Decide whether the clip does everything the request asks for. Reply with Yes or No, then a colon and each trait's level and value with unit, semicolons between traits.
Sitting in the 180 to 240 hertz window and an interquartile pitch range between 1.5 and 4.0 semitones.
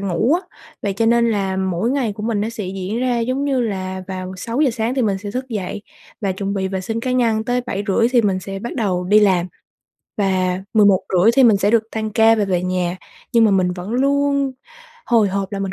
Yes: high, 210 Hz; average, 3.6 semitones